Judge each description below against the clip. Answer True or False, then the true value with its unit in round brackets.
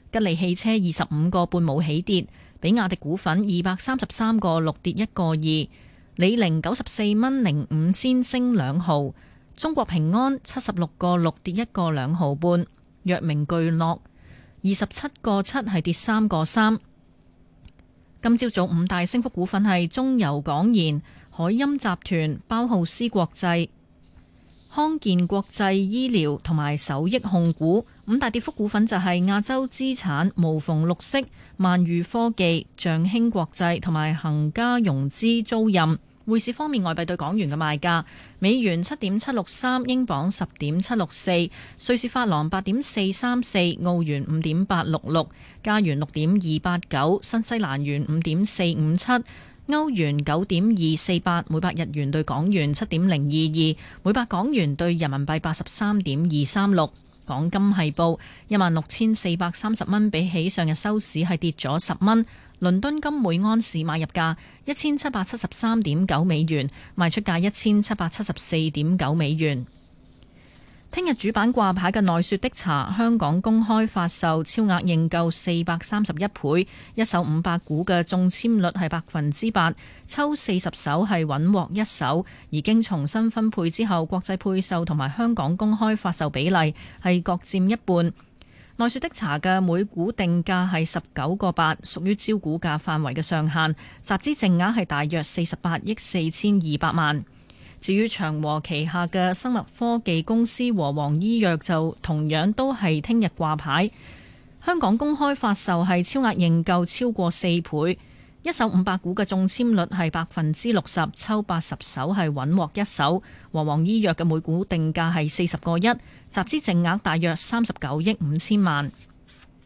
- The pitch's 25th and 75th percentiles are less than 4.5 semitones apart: False (4.8 semitones)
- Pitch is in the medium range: True (180 Hz)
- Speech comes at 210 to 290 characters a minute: True (250 characters per minute)